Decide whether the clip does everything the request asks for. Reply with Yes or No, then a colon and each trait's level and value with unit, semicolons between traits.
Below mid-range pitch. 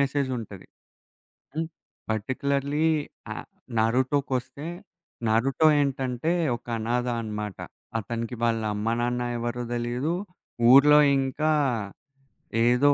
Yes: low, 125 Hz